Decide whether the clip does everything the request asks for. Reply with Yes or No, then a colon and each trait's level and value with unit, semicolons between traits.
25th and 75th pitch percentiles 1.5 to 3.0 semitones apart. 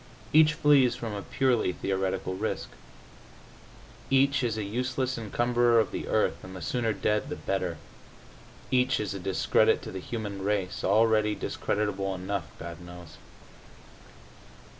No: average, 4.4 semitones